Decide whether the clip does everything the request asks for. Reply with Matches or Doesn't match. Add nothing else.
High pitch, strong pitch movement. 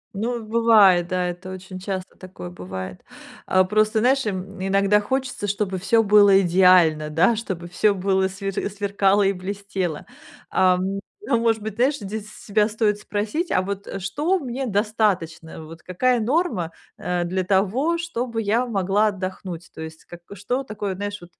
Doesn't match